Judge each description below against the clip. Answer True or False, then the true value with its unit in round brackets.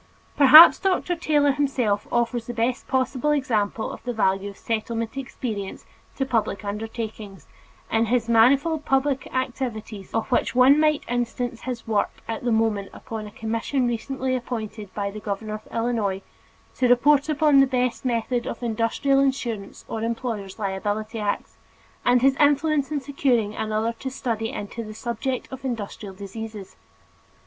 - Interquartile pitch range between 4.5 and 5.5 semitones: False (3.5 semitones)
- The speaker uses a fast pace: False (155 wpm)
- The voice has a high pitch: True (235 Hz)